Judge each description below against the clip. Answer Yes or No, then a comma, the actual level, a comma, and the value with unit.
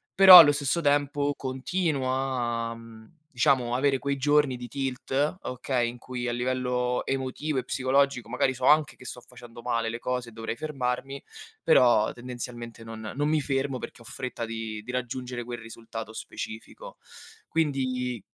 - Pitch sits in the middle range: No, low, 125 Hz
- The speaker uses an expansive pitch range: No, narrow, 2.6 semitones